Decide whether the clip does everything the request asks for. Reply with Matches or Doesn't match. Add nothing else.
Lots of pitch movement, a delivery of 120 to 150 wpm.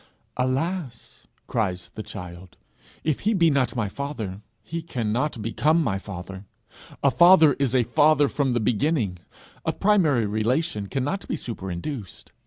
Matches